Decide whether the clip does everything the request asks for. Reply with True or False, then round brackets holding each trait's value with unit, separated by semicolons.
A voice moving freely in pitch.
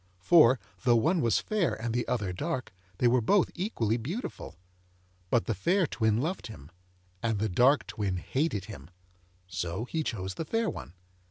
True (7.4 semitones)